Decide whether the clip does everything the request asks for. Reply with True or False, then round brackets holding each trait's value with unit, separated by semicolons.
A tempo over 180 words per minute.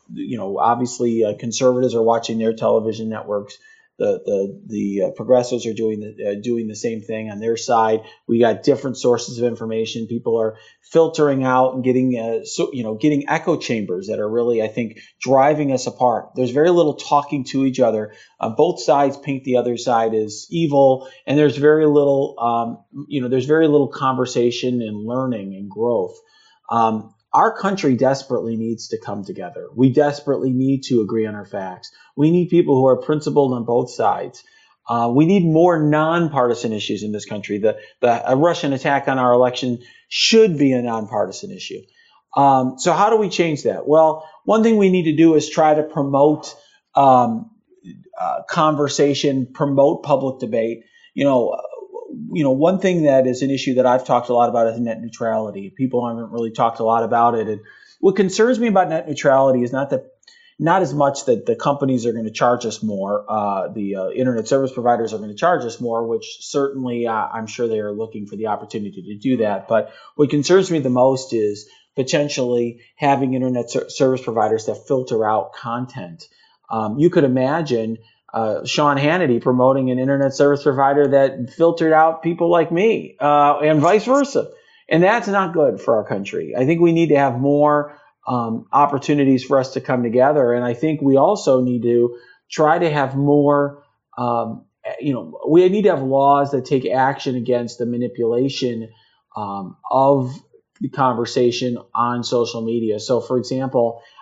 True (190 wpm)